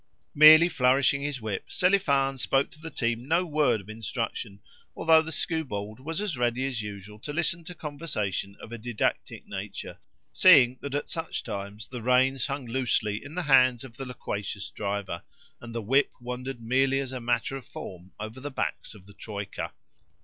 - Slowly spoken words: No, average, 180 wpm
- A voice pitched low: Yes, low, 125 Hz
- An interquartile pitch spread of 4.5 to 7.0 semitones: Yes, average, 4.9 semitones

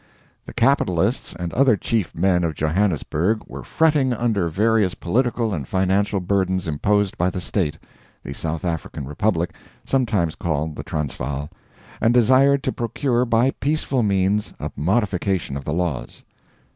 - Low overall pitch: Yes, very low, 95 Hz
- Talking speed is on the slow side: No, average, 145 wpm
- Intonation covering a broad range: Yes, wide, 5.9 semitones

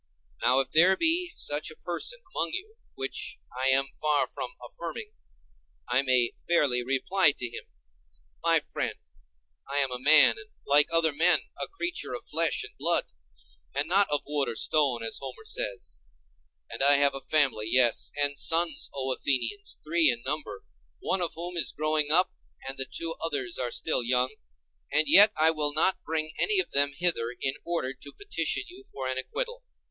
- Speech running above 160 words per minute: Yes, average, 180 wpm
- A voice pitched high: No, medium, 150 Hz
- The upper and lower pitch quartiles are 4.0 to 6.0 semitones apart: Yes, average, 4.6 semitones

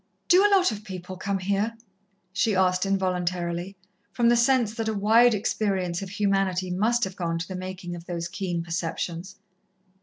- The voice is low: No, high, 190 Hz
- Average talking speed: Yes, average, 175 wpm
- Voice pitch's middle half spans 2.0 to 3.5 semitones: Yes, average, 3.1 semitones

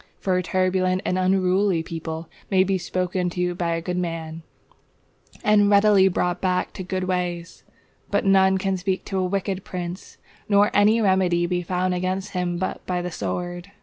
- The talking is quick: No, average, 175 wpm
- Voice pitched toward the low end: No, medium, 185 Hz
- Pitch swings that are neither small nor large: No, narrow, 1.3 semitones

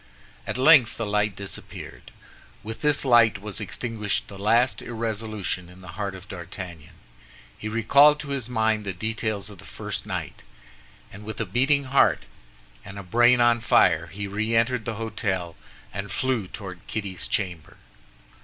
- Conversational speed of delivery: Yes, average, 160 wpm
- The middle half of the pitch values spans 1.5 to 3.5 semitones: Yes, average, 3.2 semitones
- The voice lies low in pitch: Yes, low, 110 Hz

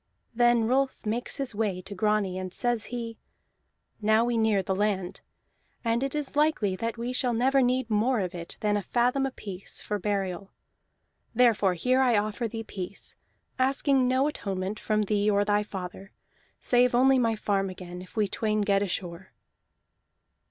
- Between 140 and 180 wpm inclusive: Yes, average, 165 wpm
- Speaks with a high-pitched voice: Yes, high, 215 Hz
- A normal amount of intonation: Yes, average, 3.8 semitones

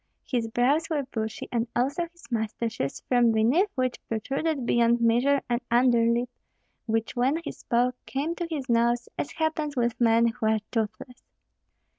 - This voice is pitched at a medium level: No, high, 245 Hz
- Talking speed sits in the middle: Yes, average, 155 wpm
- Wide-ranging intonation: No, average, 3.1 semitones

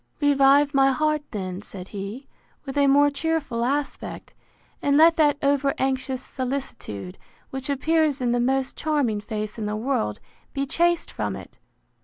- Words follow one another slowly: No, average, 155 wpm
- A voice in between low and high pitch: No, very high, 270 Hz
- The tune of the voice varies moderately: Yes, average, 3.5 semitones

